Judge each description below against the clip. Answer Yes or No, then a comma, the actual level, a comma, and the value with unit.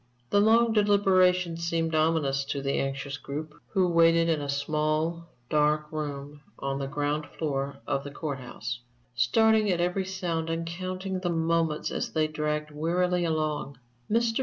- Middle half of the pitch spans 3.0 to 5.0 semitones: Yes, average, 3.6 semitones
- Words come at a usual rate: Yes, average, 160 wpm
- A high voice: No, medium, 160 Hz